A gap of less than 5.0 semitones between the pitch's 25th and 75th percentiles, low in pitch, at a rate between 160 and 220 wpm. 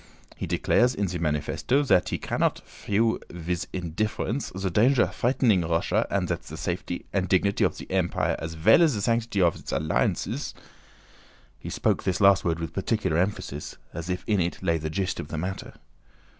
Yes: average, 4.1 semitones; very low, 90 Hz; average, 185 wpm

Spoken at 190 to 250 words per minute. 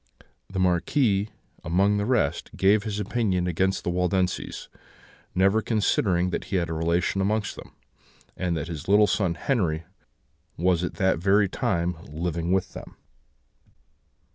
No: average, 140 wpm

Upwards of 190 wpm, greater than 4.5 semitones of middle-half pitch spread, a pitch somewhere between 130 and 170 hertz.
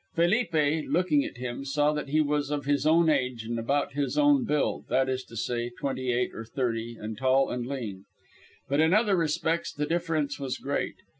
No: average, 200 wpm; average, 4.0 semitones; medium, 140 Hz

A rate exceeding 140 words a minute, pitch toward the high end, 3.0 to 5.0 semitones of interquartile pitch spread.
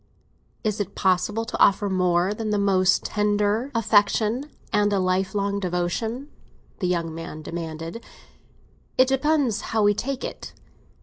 No: slow, 135 wpm; high, 205 Hz; average, 3.5 semitones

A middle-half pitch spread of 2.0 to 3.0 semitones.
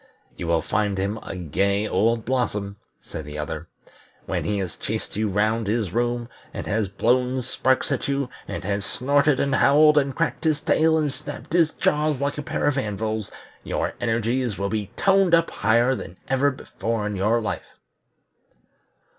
No: wide, 5.4 semitones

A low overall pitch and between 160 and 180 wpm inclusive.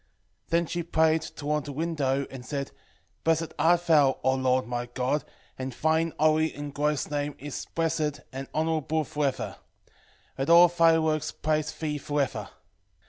No: medium, 150 Hz; average, 165 wpm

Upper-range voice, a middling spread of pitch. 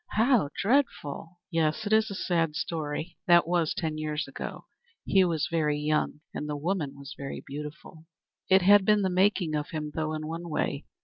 No: medium, 165 Hz; average, 3.7 semitones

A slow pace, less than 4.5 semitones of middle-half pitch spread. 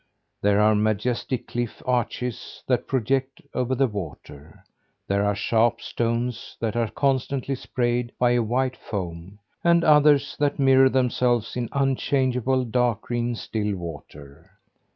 Yes: slow, 130 wpm; average, 3.6 semitones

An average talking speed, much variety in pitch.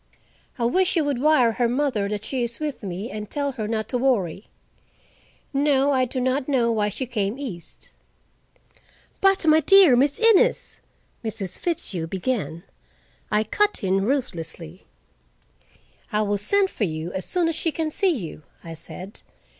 Yes: average, 160 wpm; wide, 6.3 semitones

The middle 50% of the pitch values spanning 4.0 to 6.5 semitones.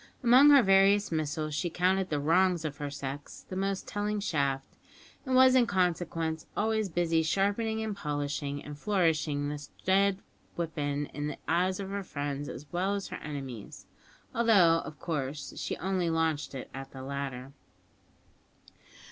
Yes: average, 5.1 semitones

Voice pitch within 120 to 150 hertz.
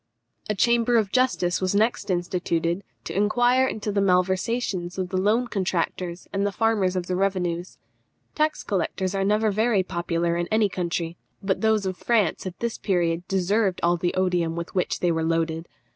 No: high, 190 Hz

